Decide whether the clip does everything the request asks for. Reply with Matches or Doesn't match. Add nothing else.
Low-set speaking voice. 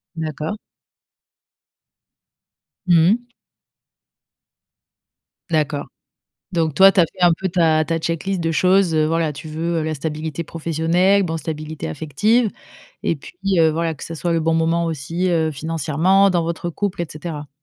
Doesn't match